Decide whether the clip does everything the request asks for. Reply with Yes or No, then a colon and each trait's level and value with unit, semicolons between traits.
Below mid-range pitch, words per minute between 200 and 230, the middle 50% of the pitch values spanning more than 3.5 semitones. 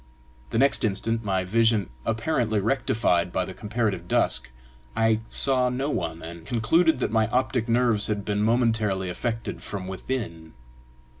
No: low, 110 Hz; average, 145 wpm; average, 3.9 semitones